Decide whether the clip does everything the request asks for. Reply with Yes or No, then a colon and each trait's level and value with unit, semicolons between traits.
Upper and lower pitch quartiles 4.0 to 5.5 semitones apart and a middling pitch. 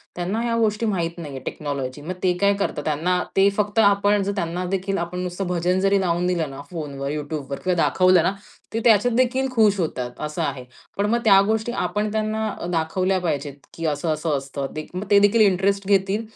Yes: average, 4.6 semitones; medium, 180 Hz